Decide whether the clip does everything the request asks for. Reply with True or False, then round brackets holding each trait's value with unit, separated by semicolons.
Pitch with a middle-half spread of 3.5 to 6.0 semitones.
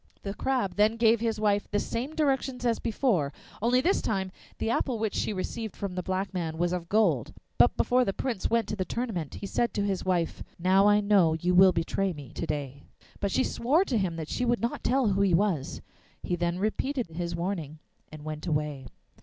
True (5.1 semitones)